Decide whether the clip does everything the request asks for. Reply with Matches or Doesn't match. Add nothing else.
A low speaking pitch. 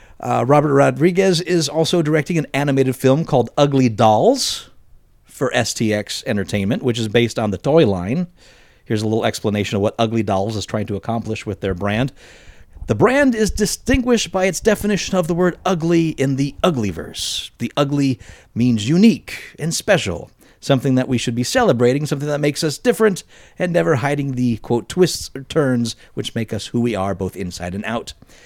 Matches